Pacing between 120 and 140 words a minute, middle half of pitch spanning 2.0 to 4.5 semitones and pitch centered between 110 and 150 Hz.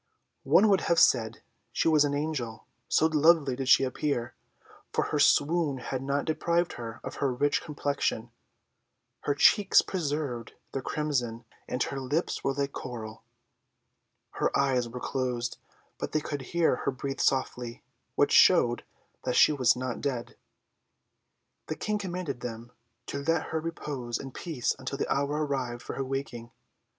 No: average, 155 wpm; average, 3.6 semitones; medium, 140 Hz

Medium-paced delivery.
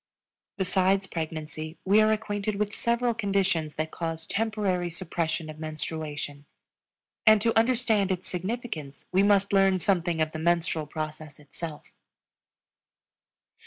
No: slow, 125 wpm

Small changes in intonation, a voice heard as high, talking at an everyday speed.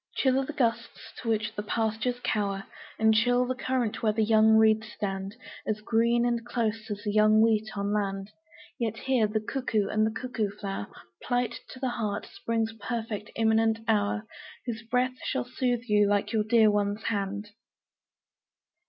Yes: narrow, 2.1 semitones; high, 220 Hz; average, 170 wpm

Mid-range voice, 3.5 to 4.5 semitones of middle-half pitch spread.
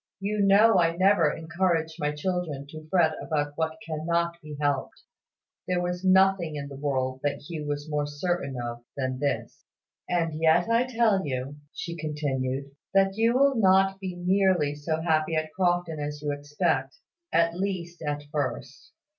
Yes: medium, 160 Hz; average, 4.1 semitones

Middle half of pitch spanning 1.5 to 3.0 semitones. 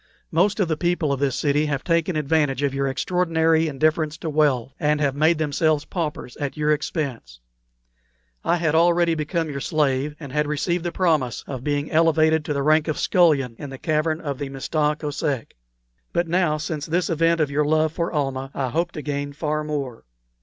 Yes: narrow, 2.4 semitones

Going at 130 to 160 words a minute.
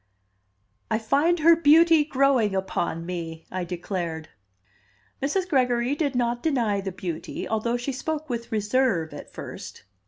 Yes: slow, 135 wpm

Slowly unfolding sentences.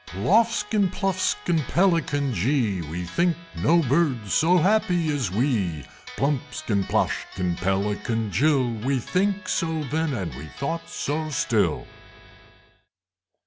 Yes: slow, 110 wpm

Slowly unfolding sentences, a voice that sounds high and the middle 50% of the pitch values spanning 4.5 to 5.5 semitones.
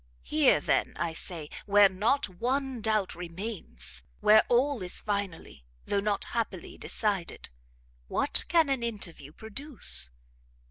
Yes: slow, 125 wpm; high, 205 Hz; average, 5.1 semitones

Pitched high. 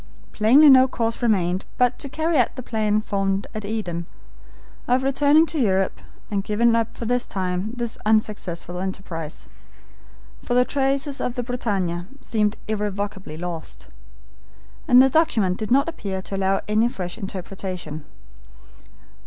Yes: high, 215 Hz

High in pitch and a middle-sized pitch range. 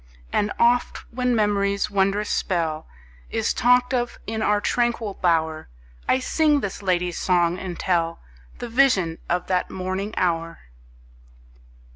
Yes: high, 200 Hz; average, 4.9 semitones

